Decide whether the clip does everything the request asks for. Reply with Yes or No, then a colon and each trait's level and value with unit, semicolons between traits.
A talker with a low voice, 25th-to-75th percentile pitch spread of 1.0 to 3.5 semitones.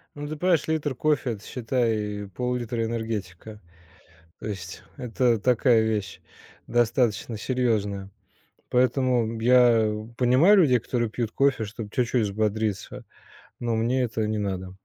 Yes: low, 115 Hz; average, 2.9 semitones